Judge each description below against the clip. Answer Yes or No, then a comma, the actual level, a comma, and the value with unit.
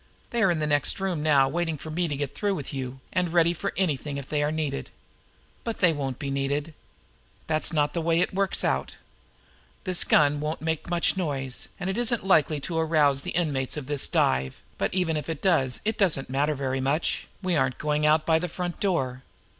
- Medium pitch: Yes, medium, 155 Hz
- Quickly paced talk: Yes, fast, 215 wpm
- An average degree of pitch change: Yes, average, 3.7 semitones